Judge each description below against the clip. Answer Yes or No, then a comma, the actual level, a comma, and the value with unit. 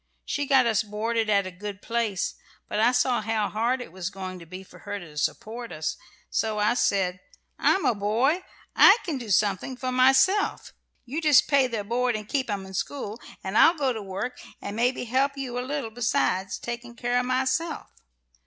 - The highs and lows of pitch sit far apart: No, average, 4.1 semitones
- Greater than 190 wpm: Yes, average, 200 wpm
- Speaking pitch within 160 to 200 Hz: No, high, 235 Hz